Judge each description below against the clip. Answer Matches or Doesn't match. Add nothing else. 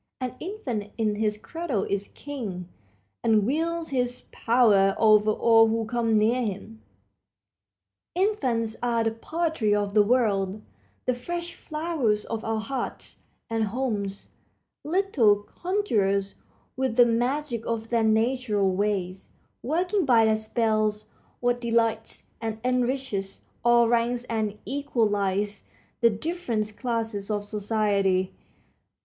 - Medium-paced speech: Doesn't match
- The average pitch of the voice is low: Doesn't match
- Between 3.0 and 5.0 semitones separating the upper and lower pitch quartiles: Matches